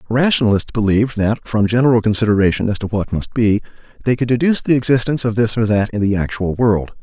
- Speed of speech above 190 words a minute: Yes, fast, 205 wpm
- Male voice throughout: Yes, male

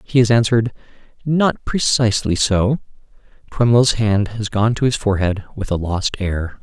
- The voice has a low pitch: Yes, low, 110 Hz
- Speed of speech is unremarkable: Yes, average, 155 wpm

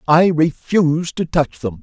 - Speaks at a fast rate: No, average, 165 wpm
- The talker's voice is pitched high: No, medium, 155 Hz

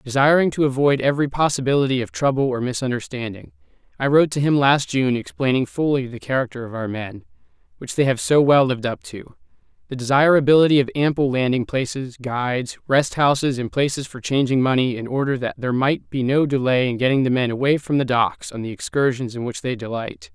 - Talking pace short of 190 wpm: No, average, 200 wpm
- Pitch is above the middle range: No, low, 130 Hz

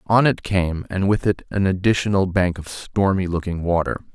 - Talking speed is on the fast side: No, average, 190 wpm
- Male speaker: Yes, male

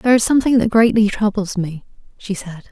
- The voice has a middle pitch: No, high, 210 Hz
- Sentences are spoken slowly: No, average, 200 wpm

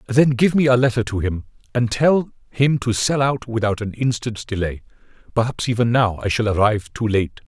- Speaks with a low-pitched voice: Yes, low, 115 Hz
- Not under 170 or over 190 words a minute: No, average, 200 wpm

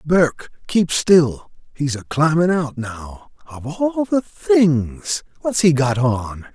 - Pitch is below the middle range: No, medium, 155 Hz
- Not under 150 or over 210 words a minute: No, slow, 135 wpm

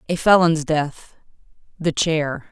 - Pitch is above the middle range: No, medium, 160 Hz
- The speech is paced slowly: Yes, slow, 95 wpm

